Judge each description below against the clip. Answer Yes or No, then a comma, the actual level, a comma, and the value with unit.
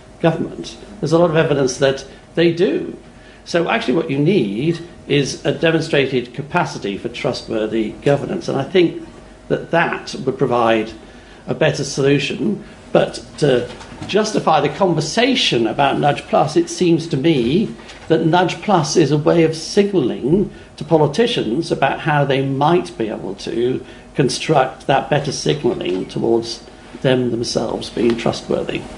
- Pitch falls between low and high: Yes, medium, 145 Hz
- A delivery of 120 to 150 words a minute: Yes, average, 145 wpm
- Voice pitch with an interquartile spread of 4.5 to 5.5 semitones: Yes, average, 5.2 semitones